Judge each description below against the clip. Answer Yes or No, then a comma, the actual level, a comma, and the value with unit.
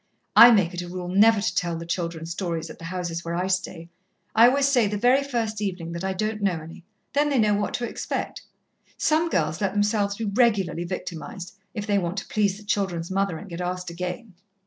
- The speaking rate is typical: No, fast, 220 wpm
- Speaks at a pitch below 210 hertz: Yes, high, 190 Hz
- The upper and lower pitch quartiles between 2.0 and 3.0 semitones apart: No, average, 3.7 semitones